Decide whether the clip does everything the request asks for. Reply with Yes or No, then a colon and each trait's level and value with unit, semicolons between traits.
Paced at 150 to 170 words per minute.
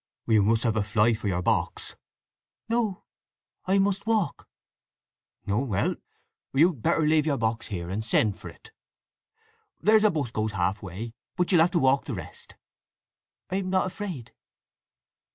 Yes: average, 160 wpm